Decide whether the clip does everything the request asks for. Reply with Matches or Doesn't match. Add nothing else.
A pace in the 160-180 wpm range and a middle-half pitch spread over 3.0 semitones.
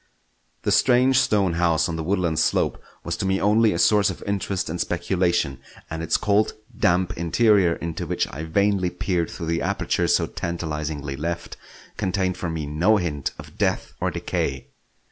Matches